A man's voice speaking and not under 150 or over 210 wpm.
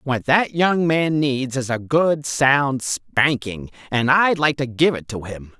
Yes: male; average, 195 wpm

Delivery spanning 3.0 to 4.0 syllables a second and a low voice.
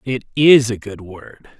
Yes: 3.7 syllables/s; low, 115 Hz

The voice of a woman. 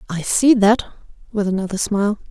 Yes: female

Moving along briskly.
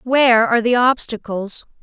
No: slow, 130 wpm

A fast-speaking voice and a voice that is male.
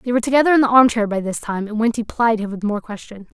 No: fast, 285 wpm; female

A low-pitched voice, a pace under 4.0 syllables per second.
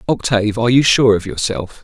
No: low, 115 Hz; 6.0 syllables/s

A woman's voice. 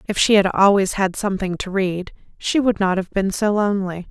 Yes: female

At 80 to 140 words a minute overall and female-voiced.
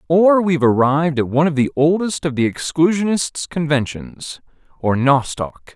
No: slow, 135 wpm; male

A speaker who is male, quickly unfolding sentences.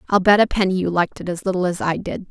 No: female; fast, 315 wpm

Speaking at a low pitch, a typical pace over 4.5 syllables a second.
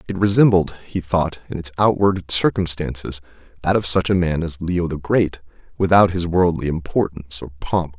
Yes: very low, 85 Hz; 4.9 syllables/s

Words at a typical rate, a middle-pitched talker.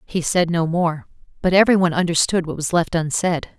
Yes: average, 185 wpm; medium, 170 Hz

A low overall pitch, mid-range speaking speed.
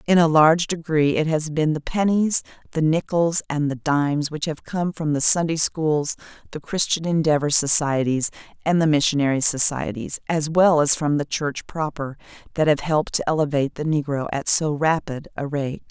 No: medium, 155 Hz; average, 180 wpm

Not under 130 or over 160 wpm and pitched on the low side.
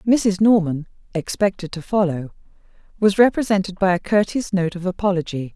No: average, 140 wpm; high, 190 Hz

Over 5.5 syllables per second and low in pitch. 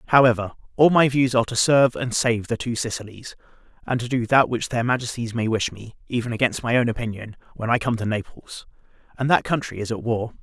Yes: 6.1 syllables/s; low, 120 Hz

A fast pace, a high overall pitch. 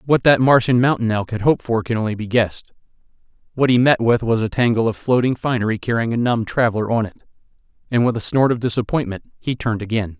No: fast, 220 wpm; low, 115 Hz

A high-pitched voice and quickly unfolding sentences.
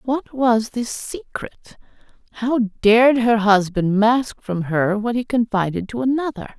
No: high, 230 Hz; average, 145 wpm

